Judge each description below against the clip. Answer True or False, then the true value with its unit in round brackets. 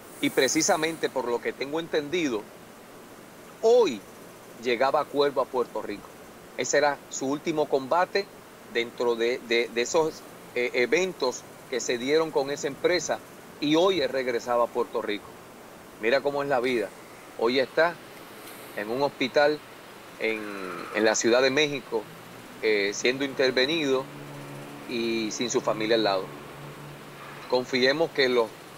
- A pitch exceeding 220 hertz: False (135 Hz)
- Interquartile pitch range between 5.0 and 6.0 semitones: True (5.6 semitones)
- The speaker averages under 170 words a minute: True (140 wpm)